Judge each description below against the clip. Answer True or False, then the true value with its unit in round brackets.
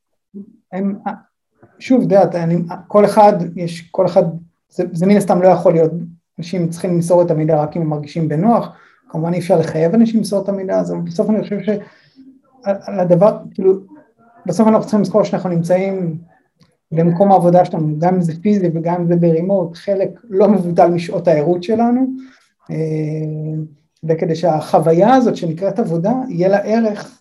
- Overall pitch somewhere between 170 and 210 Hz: True (185 Hz)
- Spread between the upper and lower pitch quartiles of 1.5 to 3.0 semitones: False (3.4 semitones)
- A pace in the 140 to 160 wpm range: True (155 wpm)